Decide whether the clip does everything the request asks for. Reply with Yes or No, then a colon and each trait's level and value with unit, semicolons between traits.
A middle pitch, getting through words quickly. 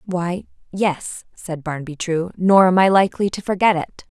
No: medium, 180 Hz; average, 170 wpm